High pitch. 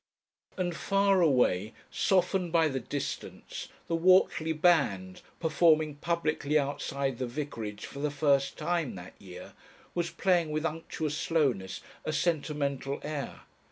No: medium, 150 Hz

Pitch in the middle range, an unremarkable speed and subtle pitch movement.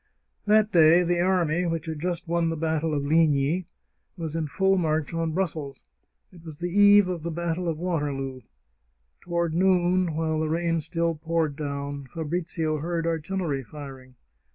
Yes: medium, 165 Hz; average, 160 wpm; narrow, 2.3 semitones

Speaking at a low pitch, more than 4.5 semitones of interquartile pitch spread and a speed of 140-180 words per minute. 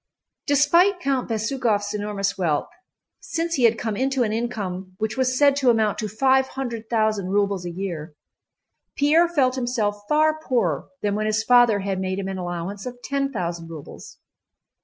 No: high, 220 Hz; average, 5.1 semitones; average, 170 wpm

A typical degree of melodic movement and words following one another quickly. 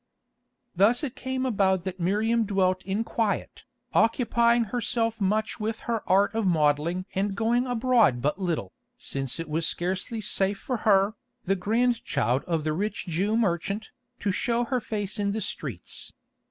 No: average, 3.9 semitones; average, 155 wpm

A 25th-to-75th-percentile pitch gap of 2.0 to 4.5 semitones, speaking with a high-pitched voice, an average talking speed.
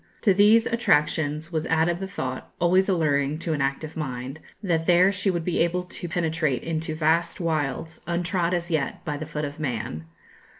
No: average, 2.8 semitones; medium, 160 Hz; average, 180 wpm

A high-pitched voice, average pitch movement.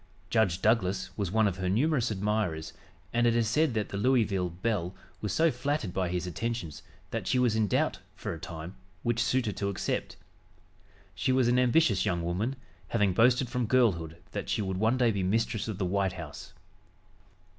No: low, 105 Hz; average, 4.3 semitones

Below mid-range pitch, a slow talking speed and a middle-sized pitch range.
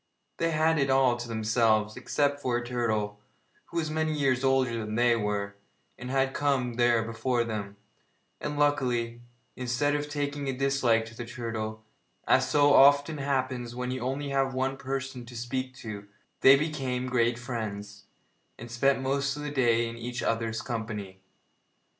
No: low, 125 Hz; average, 165 wpm; average, 3.0 semitones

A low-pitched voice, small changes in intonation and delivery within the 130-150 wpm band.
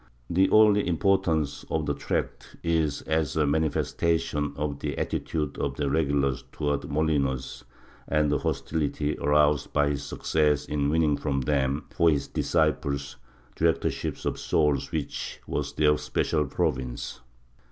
Yes: very low, 75 Hz; narrow, 2.0 semitones; average, 140 wpm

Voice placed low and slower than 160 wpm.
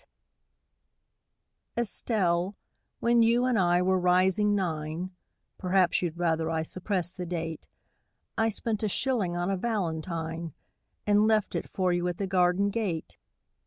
No: medium, 185 Hz; average, 140 wpm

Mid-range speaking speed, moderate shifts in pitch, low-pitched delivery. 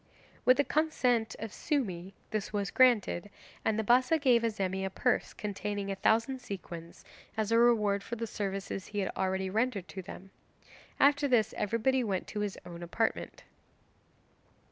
No: average, 160 wpm; average, 3.8 semitones; high, 210 Hz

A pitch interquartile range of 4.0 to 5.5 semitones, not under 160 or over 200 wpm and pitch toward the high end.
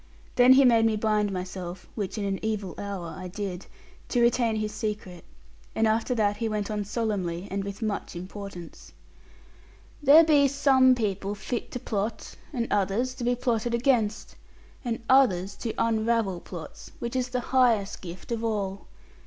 No: average, 3.4 semitones; average, 165 wpm; high, 215 Hz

